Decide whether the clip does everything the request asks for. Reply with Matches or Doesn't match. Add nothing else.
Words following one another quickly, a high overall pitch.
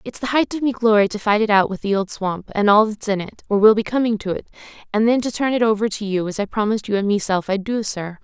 Matches